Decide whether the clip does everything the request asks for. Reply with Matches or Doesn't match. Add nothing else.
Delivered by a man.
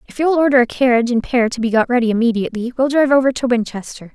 Doesn't match